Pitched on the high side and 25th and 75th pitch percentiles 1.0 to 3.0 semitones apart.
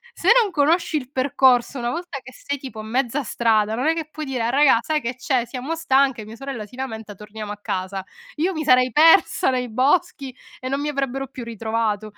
No: very high, 255 Hz; average, 3.9 semitones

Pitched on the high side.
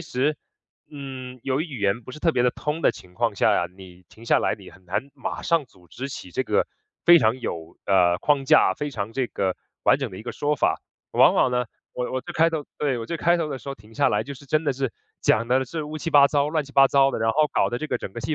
No: low, 130 Hz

